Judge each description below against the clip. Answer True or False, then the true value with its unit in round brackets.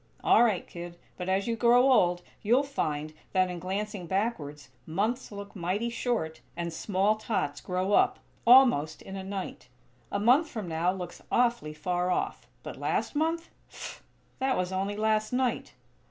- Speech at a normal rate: True (165 wpm)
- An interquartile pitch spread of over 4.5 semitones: True (5.0 semitones)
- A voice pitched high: True (195 Hz)